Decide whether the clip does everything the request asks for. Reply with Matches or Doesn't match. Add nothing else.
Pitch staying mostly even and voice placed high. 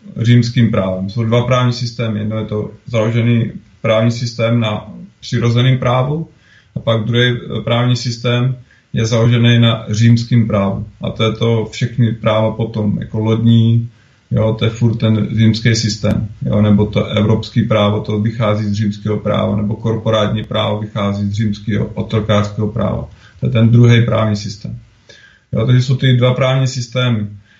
Doesn't match